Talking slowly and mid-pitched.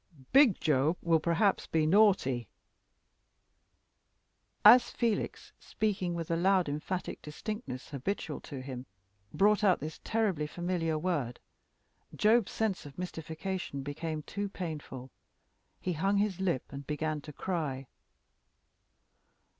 Yes: slow, 120 wpm; medium, 170 Hz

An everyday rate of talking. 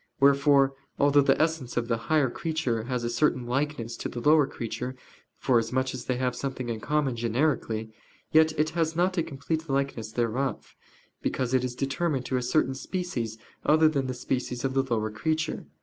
Yes: average, 180 wpm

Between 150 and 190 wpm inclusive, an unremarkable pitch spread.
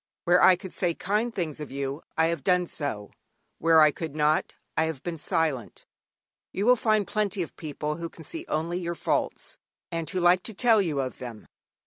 No: average, 200 wpm; average, 3.5 semitones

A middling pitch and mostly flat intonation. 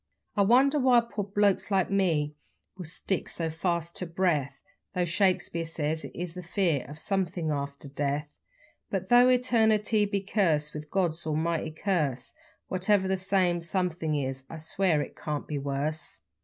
No: medium, 175 Hz; average, 4.3 semitones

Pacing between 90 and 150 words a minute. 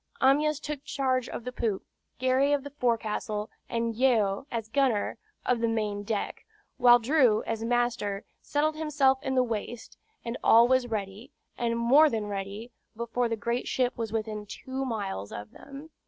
No: average, 170 wpm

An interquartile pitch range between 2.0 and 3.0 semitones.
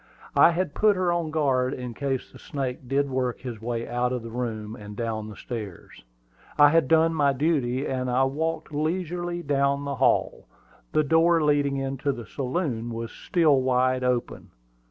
No: average, 4.0 semitones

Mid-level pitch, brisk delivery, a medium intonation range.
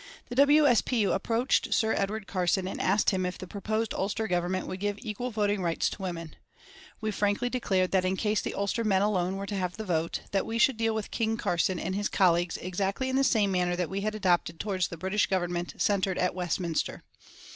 No: high, 195 Hz; fast, 220 wpm; average, 3.0 semitones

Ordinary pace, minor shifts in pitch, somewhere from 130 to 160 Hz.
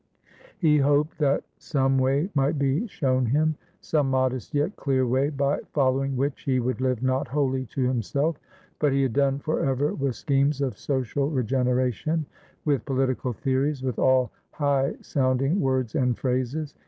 Yes: average, 160 wpm; narrow, 1.9 semitones; low, 135 Hz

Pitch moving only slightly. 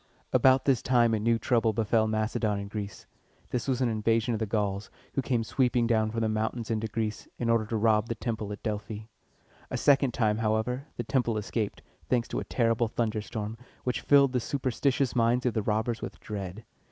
Yes: narrow, 2.1 semitones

